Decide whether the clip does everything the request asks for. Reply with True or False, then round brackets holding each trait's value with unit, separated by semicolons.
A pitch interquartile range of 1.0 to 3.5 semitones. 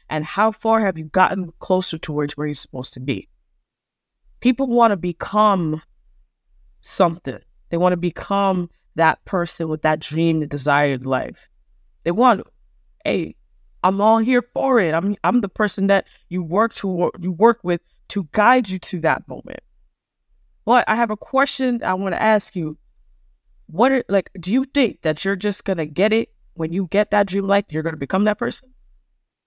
False (5.2 semitones)